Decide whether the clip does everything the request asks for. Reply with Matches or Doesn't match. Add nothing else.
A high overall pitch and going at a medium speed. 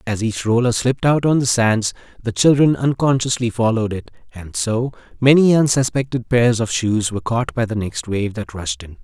Doesn't match